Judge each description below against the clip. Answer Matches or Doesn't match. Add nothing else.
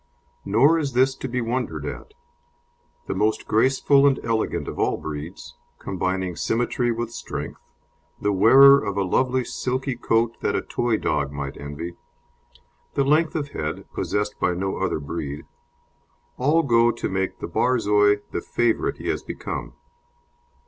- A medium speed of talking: Matches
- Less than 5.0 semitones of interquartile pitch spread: Doesn't match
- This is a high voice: Doesn't match